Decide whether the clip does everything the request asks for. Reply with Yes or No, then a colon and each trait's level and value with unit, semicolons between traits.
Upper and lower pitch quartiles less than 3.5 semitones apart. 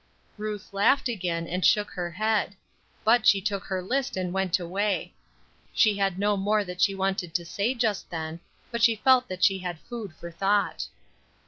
Yes: average, 2.9 semitones